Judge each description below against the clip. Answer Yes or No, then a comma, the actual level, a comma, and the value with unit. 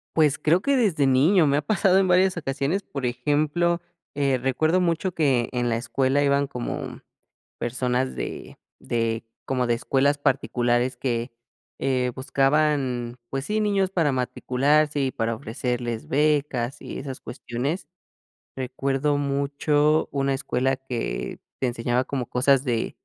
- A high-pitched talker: No, low, 135 Hz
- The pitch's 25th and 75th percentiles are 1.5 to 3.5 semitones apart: Yes, average, 3.2 semitones